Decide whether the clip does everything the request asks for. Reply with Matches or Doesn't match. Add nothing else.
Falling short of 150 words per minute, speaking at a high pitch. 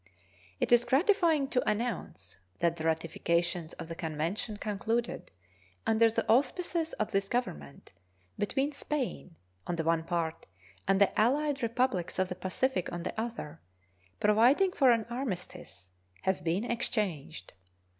Matches